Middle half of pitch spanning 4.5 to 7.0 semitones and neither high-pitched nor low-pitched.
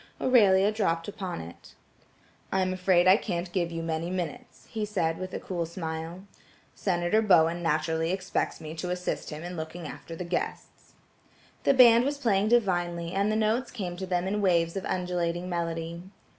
No: average, 2.8 semitones; medium, 180 Hz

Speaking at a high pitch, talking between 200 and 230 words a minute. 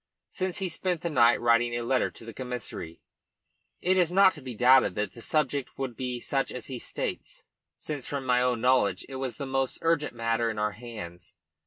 No: low, 125 Hz; fast, 205 wpm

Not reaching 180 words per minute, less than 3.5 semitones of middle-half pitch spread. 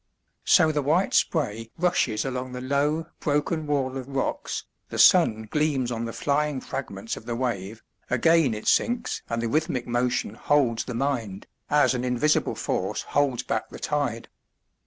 No: average, 160 wpm; average, 4.1 semitones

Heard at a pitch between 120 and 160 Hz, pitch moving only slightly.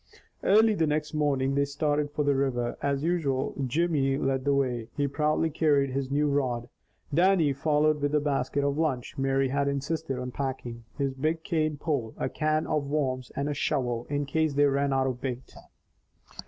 Yes: medium, 140 Hz; narrow, 2.2 semitones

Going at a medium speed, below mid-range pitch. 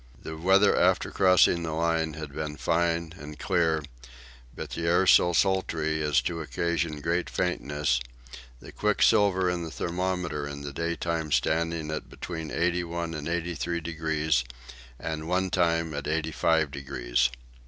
Yes: average, 145 wpm; very low, 80 Hz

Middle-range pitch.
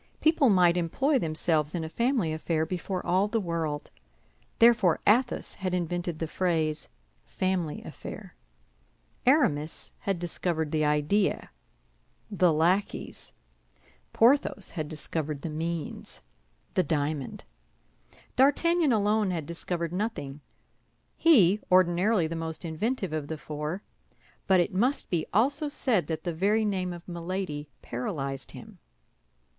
Yes: medium, 175 Hz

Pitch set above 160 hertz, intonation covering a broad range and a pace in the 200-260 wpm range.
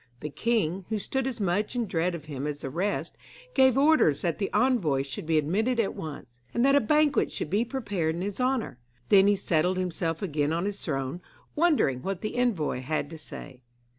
Yes: medium, 185 Hz; wide, 7.2 semitones; fast, 205 wpm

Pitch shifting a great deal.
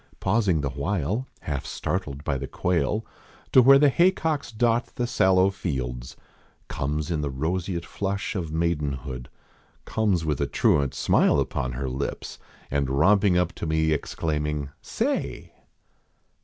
Yes: wide, 6.0 semitones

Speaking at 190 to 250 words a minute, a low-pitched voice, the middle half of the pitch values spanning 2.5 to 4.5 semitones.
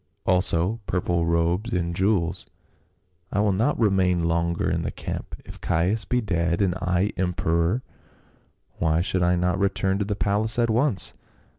No: average, 155 wpm; very low, 90 Hz; average, 3.3 semitones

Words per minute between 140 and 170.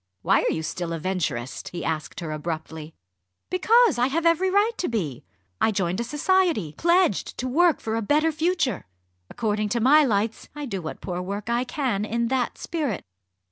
No: average, 185 wpm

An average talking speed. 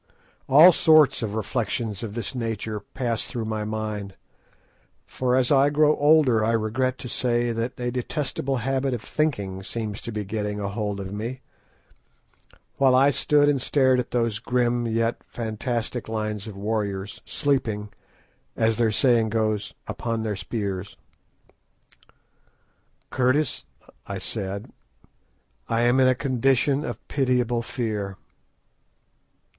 No: slow, 130 wpm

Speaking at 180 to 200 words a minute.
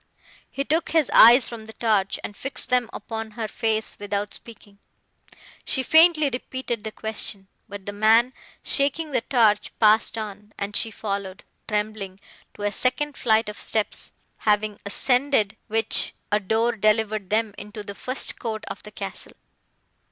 No: average, 155 wpm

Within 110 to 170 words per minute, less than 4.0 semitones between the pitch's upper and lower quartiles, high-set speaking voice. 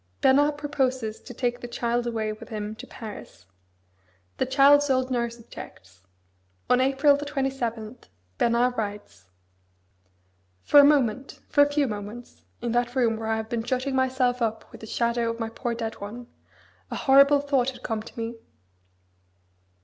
Yes: average, 165 wpm; average, 3.0 semitones; high, 240 Hz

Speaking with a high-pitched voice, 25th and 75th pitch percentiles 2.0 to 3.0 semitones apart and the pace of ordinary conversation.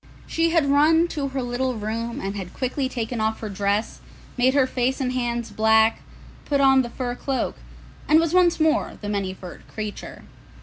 No: very high, 250 Hz; average, 4.1 semitones; average, 185 wpm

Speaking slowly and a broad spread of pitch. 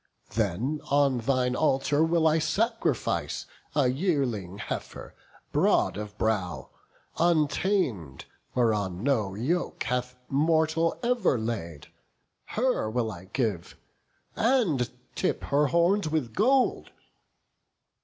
Yes: slow, 105 wpm; wide, 6.8 semitones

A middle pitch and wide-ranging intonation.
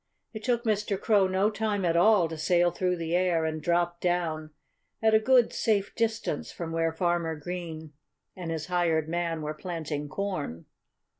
No: medium, 175 Hz; average, 3.6 semitones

